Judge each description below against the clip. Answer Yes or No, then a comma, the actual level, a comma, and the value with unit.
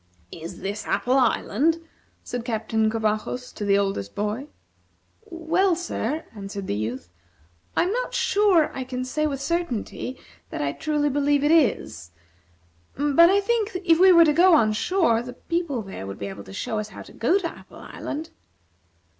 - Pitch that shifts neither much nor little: No, wide, 7.9 semitones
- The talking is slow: No, average, 180 wpm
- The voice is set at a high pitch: Yes, very high, 265 Hz